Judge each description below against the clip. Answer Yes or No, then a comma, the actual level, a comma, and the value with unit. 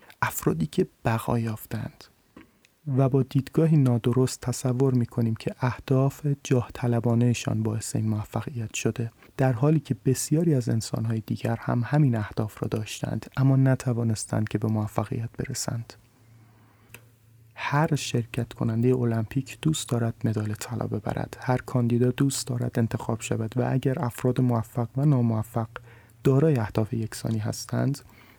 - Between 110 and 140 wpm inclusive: Yes, average, 130 wpm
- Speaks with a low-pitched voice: Yes, low, 120 Hz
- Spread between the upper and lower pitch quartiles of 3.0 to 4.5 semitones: No, narrow, 2.6 semitones